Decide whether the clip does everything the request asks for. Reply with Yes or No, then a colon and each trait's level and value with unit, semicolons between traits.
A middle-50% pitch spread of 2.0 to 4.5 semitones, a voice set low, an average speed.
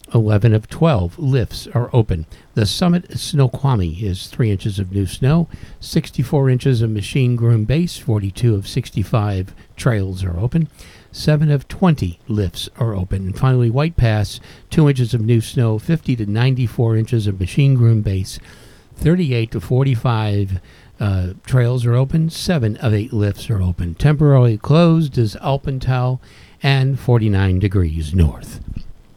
No: average, 5.0 semitones; low, 115 Hz; average, 145 wpm